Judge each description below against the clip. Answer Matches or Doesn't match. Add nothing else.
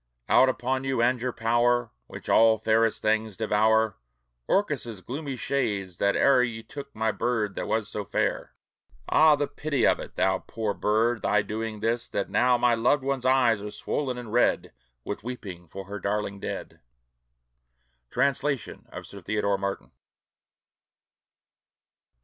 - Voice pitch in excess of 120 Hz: Doesn't match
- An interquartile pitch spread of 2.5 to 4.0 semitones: Matches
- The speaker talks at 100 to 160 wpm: Matches